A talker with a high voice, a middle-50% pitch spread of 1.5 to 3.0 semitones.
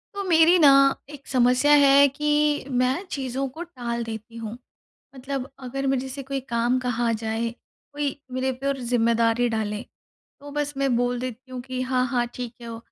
Yes: very high, 255 Hz; narrow, 2.6 semitones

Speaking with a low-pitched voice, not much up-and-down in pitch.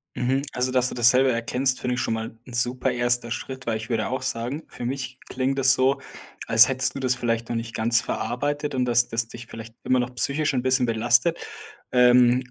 Yes: low, 125 Hz; narrow, 1.9 semitones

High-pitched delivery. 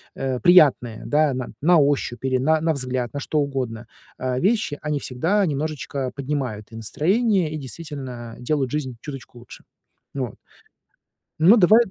No: medium, 140 Hz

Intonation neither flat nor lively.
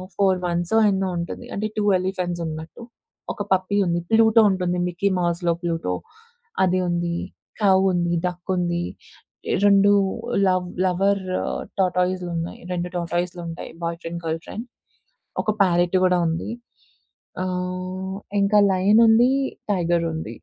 No: narrow, 1.9 semitones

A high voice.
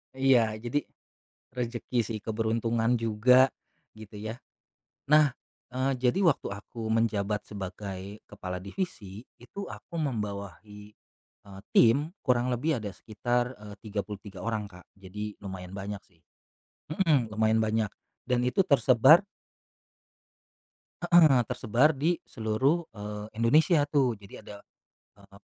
No: low, 115 Hz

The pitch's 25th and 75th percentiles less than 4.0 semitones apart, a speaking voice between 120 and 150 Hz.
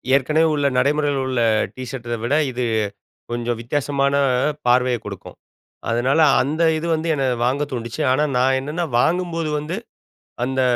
Yes: average, 3.4 semitones; low, 135 Hz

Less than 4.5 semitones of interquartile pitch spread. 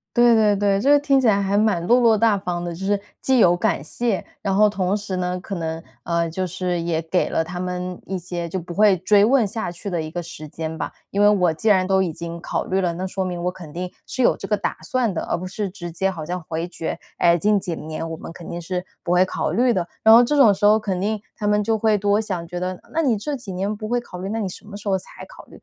Yes: average, 3.4 semitones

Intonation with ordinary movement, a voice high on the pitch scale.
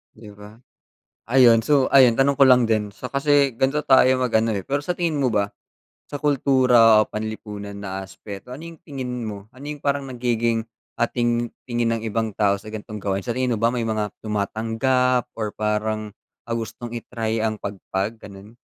No: average, 3.3 semitones; low, 115 Hz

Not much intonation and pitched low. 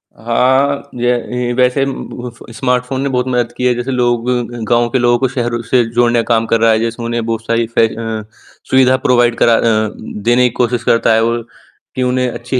Yes: narrow, 1.4 semitones; low, 120 Hz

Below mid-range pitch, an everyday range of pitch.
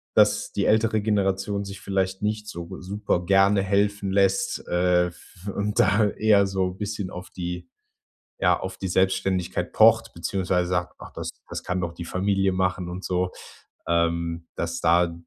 No: very low, 95 Hz; narrow, 2.2 semitones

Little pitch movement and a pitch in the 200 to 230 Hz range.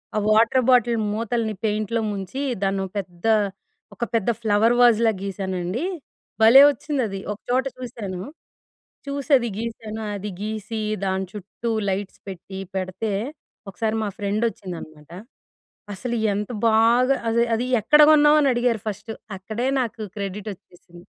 No: average, 3.4 semitones; high, 220 Hz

